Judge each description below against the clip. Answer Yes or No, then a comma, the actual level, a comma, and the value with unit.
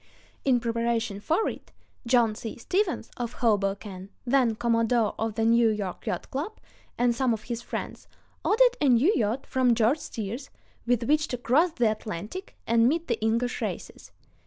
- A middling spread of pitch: Yes, average, 3.0 semitones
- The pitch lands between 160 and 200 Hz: No, high, 235 Hz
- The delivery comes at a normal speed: Yes, average, 165 wpm